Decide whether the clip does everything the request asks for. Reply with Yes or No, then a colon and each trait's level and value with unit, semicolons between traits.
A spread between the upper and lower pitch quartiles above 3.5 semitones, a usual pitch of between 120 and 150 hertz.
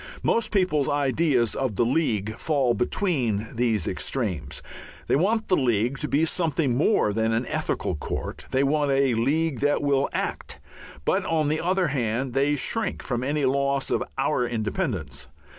Yes: average, 4.7 semitones; low, 135 Hz